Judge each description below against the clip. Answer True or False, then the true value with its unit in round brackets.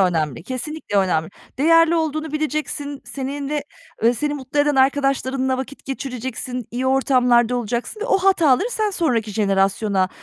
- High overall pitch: True (265 Hz)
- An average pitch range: True (4.1 semitones)